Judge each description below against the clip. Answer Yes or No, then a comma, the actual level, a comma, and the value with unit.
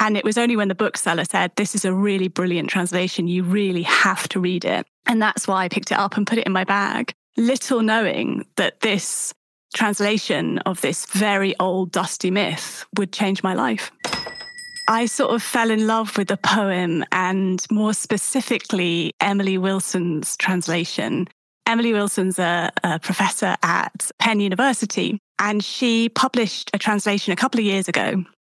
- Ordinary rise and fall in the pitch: Yes, average, 3.0 semitones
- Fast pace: No, average, 170 wpm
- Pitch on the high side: Yes, high, 205 Hz